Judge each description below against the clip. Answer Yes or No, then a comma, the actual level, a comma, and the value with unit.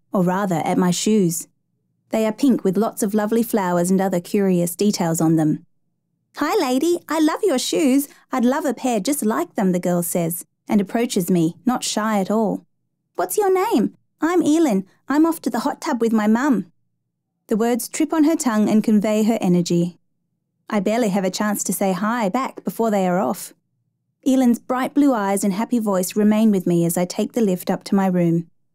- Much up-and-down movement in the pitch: Yes, wide, 5.7 semitones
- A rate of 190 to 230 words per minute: Yes, fast, 205 wpm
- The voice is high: Yes, high, 210 Hz